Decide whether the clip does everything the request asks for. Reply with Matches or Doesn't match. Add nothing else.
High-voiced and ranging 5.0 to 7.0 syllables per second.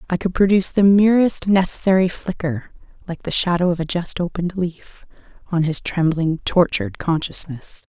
Doesn't match